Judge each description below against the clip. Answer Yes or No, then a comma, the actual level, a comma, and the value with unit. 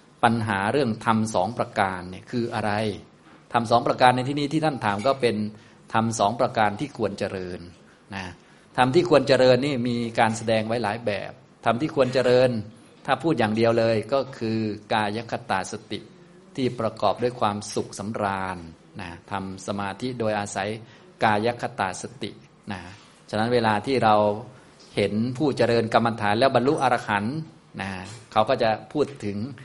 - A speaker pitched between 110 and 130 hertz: Yes, low, 115 Hz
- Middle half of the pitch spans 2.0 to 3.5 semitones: Yes, average, 3.2 semitones